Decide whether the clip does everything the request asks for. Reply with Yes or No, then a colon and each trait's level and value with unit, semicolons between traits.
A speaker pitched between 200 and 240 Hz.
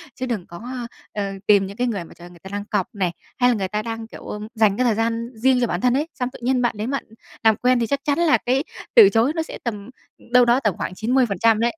Yes: high, 230 Hz